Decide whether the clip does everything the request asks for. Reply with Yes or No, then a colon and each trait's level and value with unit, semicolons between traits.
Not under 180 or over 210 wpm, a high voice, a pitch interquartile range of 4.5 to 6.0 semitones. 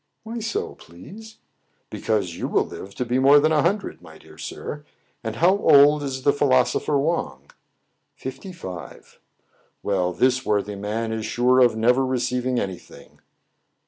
No: average, 185 wpm; low, 130 Hz; average, 5.3 semitones